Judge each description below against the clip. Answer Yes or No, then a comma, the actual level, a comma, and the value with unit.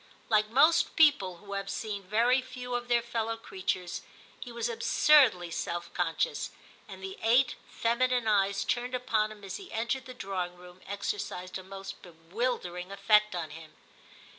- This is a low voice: No, high, 215 Hz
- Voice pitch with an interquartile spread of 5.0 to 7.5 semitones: No, average, 4.6 semitones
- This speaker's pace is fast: No, average, 165 wpm